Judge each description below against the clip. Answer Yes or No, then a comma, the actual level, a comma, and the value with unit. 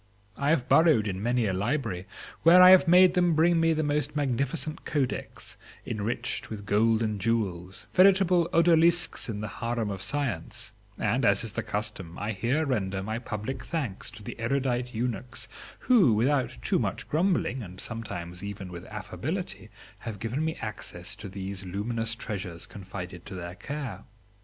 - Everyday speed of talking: Yes, average, 160 wpm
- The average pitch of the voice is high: No, low, 115 Hz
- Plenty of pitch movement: Yes, wide, 6.6 semitones